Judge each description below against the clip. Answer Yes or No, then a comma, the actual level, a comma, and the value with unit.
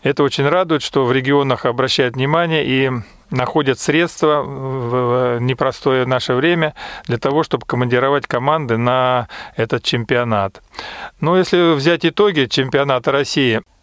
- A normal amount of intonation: Yes, average, 3.3 semitones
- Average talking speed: Yes, average, 125 wpm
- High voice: No, low, 135 Hz